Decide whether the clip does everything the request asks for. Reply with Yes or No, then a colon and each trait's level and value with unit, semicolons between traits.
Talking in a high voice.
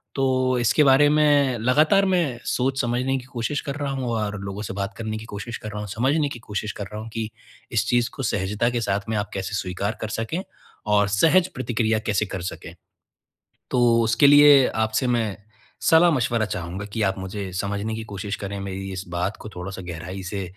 No: low, 110 Hz